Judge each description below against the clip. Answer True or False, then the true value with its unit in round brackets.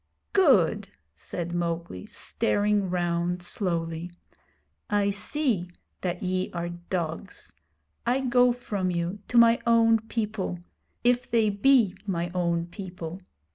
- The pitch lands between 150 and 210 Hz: True (185 Hz)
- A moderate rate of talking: False (115 wpm)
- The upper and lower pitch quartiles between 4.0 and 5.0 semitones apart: True (4.5 semitones)